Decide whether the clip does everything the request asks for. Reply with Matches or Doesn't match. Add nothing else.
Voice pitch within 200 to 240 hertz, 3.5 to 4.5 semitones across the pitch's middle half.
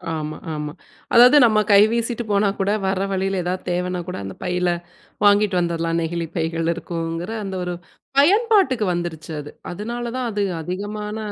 Doesn't match